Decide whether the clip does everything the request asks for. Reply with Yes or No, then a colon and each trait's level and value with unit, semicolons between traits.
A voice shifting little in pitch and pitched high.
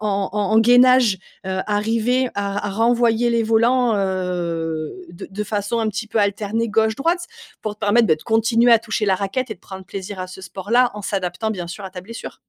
No: average, 3.2 semitones; high, 210 Hz